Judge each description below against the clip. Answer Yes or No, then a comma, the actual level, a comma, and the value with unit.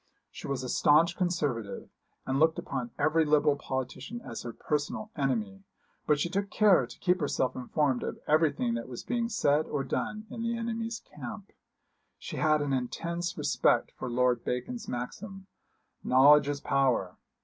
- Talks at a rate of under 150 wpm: No, average, 160 wpm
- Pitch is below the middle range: No, medium, 145 Hz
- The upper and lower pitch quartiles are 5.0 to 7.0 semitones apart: Yes, wide, 5.5 semitones